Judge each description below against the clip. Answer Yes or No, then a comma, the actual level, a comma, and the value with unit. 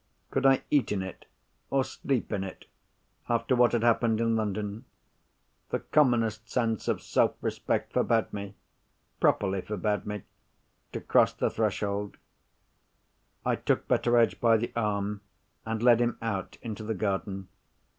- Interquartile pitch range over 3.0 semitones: No, narrow, 2.6 semitones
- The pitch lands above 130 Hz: No, low, 110 Hz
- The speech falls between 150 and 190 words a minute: No, slow, 135 wpm